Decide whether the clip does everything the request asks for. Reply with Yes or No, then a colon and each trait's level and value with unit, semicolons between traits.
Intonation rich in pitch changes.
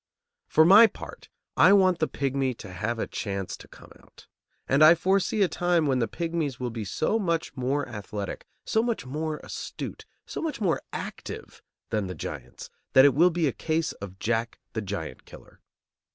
Yes: wide, 7.1 semitones